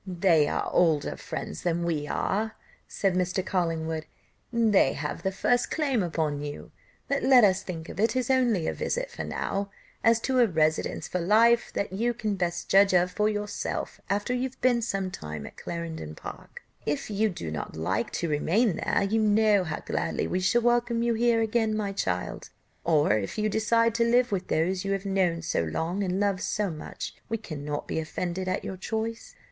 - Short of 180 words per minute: No, average, 195 wpm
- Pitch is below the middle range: No, high, 195 Hz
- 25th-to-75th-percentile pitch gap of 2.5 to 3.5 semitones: No, average, 5.3 semitones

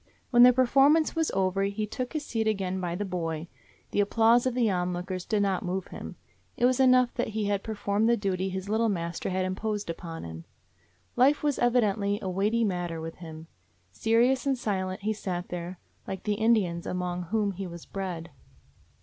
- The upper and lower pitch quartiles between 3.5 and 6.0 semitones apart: Yes, average, 4.0 semitones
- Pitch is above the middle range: Yes, high, 200 Hz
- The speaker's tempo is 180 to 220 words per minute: Yes, average, 195 wpm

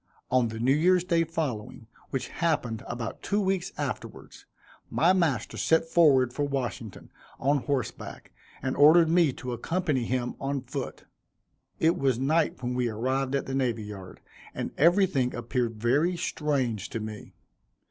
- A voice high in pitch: No, low, 135 Hz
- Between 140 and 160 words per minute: Yes, average, 150 wpm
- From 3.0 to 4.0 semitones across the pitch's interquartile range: No, average, 5.1 semitones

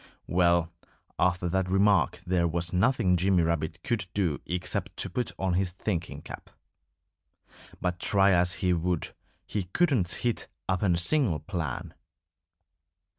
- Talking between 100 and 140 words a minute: Yes, slow, 135 wpm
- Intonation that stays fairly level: Yes, narrow, 2.2 semitones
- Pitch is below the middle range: Yes, very low, 90 Hz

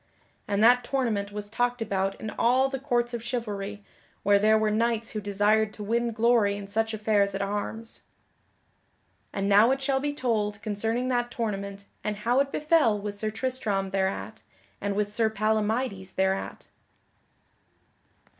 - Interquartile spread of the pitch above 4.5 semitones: No, average, 2.8 semitones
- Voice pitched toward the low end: No, high, 215 Hz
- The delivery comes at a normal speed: Yes, average, 155 wpm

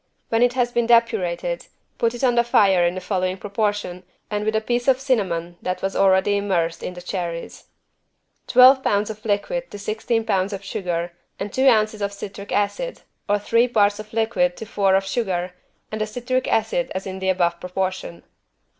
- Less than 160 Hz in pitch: No, high, 205 Hz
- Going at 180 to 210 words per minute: Yes, average, 190 wpm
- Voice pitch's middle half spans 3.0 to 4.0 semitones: Yes, average, 3.6 semitones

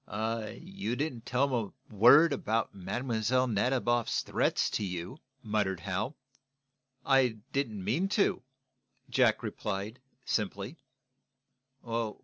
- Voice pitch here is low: Yes, low, 115 Hz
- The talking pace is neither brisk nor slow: No, slow, 105 wpm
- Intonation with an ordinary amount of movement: Yes, average, 4.3 semitones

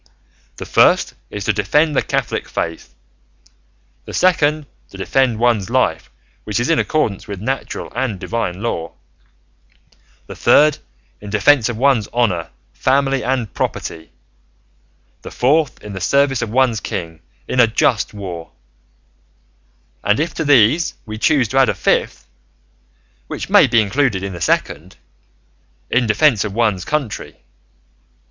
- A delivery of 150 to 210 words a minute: No, average, 140 wpm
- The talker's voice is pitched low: Yes, low, 115 Hz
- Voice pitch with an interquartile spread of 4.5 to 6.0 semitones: Yes, average, 5.2 semitones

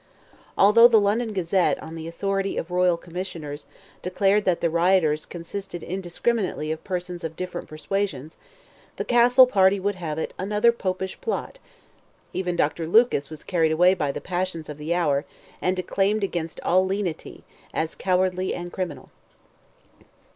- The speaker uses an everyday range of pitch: Yes, average, 3.0 semitones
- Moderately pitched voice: Yes, medium, 180 Hz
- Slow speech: No, average, 150 wpm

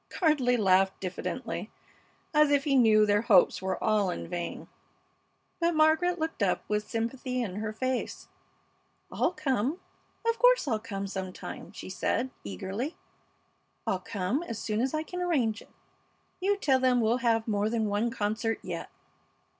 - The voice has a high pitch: Yes, high, 230 Hz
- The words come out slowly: No, average, 160 wpm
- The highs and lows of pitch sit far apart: Yes, wide, 5.8 semitones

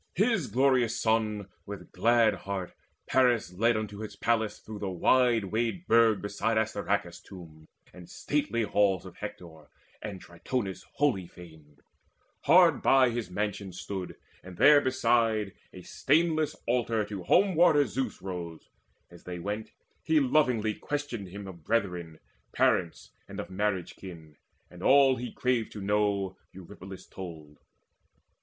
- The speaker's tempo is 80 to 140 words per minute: Yes, slow, 135 wpm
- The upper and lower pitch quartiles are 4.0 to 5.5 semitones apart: Yes, average, 4.5 semitones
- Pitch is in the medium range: No, low, 105 Hz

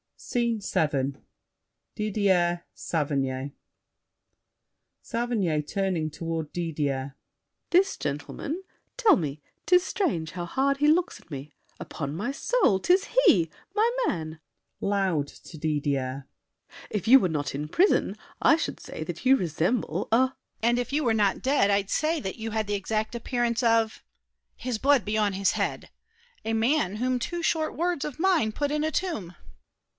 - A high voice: Yes, high, 215 Hz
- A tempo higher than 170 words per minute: No, average, 150 wpm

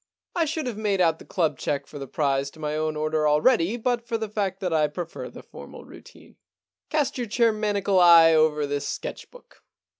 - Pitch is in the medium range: Yes, medium, 175 Hz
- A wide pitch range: Yes, wide, 6.5 semitones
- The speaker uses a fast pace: Yes, fast, 210 wpm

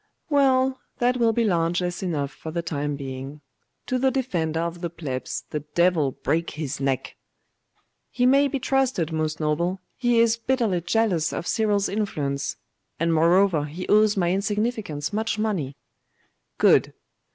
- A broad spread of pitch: Yes, wide, 6.5 semitones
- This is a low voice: No, medium, 175 Hz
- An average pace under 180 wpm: Yes, average, 150 wpm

